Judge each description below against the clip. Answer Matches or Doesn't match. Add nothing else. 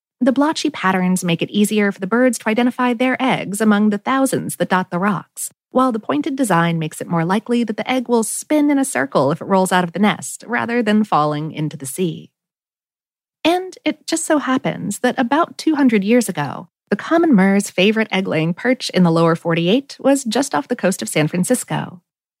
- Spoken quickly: Matches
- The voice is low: Doesn't match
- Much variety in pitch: Matches